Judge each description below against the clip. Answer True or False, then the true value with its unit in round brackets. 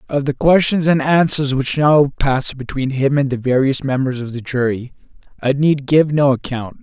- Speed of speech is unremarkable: True (195 wpm)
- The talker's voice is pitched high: False (135 Hz)